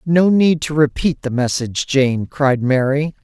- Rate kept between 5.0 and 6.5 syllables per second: No, 4.2 syllables/s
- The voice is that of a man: Yes, male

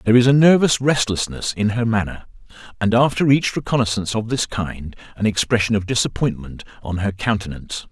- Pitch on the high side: No, low, 110 Hz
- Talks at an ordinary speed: Yes, average, 165 wpm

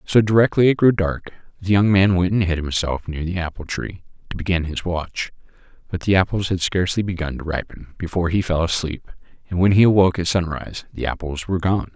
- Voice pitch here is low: Yes, very low, 90 Hz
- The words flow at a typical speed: No, fast, 210 wpm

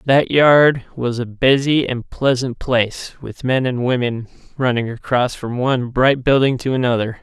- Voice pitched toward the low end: Yes, low, 125 Hz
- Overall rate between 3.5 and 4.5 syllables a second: Yes, 4.4 syllables/s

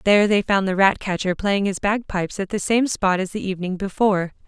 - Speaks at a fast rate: Yes, fast, 215 wpm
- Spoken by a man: No, female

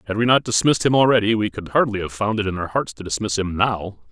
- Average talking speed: No, fast, 275 wpm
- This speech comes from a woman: No, male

